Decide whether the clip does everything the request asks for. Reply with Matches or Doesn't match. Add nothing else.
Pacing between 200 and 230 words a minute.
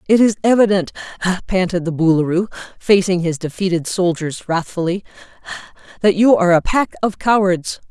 Doesn't match